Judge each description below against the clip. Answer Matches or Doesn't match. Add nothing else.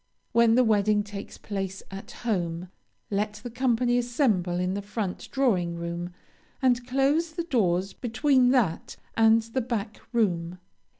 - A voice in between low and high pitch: Doesn't match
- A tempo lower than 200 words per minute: Matches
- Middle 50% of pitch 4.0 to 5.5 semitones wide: Matches